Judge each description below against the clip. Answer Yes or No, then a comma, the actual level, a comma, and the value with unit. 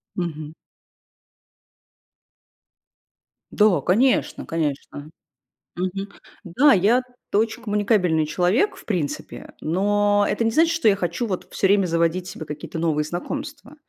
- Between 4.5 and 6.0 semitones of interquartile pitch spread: Yes, average, 5.2 semitones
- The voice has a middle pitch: No, high, 195 Hz